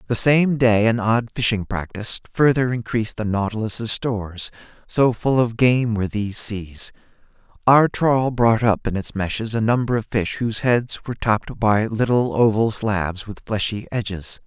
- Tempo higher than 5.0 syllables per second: No, 4.7 syllables/s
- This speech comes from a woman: No, male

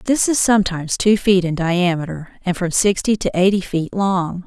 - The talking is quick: No, average, 190 wpm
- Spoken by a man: No, female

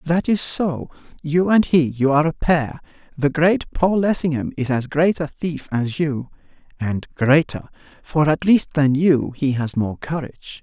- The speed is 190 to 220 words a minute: No, average, 160 wpm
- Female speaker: No, male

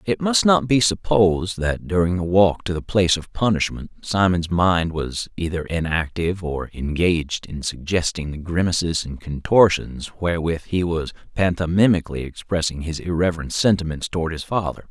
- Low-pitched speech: Yes, very low, 85 Hz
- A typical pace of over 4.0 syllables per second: Yes, 5.1 syllables/s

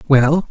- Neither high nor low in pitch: Yes, medium, 145 Hz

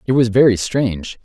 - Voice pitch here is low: Yes, low, 115 Hz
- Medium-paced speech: Yes, average, 195 wpm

